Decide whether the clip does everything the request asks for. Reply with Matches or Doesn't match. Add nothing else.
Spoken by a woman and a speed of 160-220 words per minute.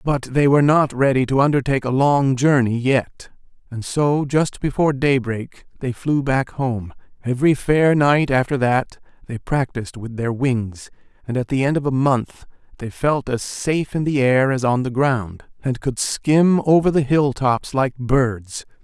Doesn't match